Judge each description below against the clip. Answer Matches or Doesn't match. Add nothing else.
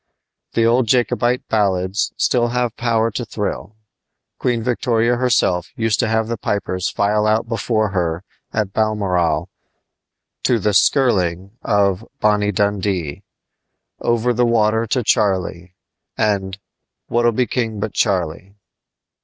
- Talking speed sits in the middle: Doesn't match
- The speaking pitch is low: Matches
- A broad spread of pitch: Doesn't match